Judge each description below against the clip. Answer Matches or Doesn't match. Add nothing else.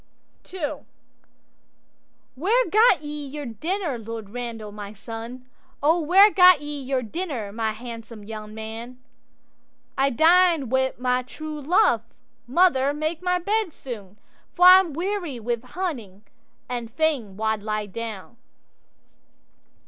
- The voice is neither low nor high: Doesn't match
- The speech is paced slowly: Matches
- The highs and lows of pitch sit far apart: Matches